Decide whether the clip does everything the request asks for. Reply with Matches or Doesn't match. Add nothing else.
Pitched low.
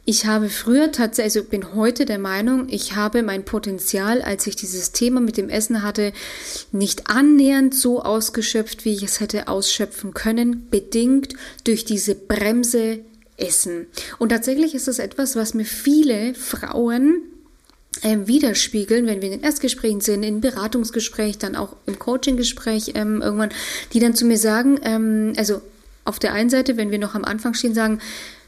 Doesn't match